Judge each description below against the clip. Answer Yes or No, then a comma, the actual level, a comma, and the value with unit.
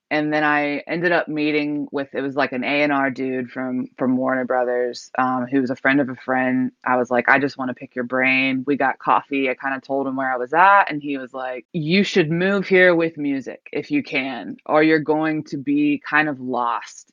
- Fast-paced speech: Yes, fast, 240 wpm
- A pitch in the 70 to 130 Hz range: No, medium, 140 Hz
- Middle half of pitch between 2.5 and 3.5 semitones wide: Yes, average, 2.8 semitones